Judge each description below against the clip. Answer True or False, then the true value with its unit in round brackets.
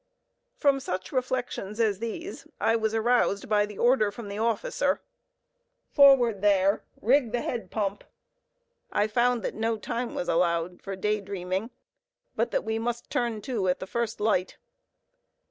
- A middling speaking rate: True (155 wpm)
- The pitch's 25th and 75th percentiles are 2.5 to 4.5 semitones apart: True (3.1 semitones)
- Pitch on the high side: True (220 Hz)